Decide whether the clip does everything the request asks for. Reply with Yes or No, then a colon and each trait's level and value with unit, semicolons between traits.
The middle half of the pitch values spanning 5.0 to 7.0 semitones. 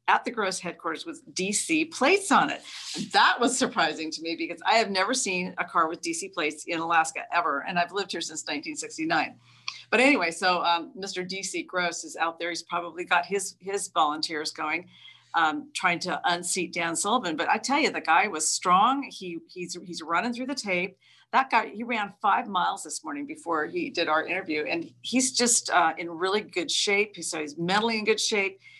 Yes: wide, 5.4 semitones